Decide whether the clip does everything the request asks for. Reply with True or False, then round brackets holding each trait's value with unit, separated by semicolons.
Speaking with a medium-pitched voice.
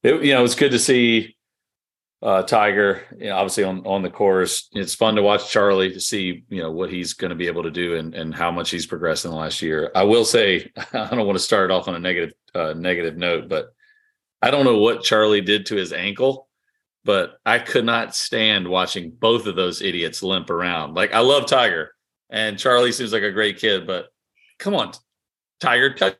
False (105 Hz)